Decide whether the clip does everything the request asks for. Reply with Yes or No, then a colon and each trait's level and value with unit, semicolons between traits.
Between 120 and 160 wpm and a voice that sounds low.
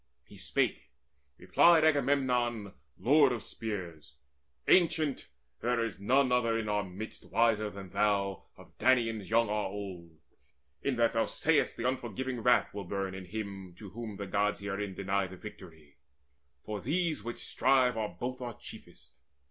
Yes: average, 155 wpm; low, 110 Hz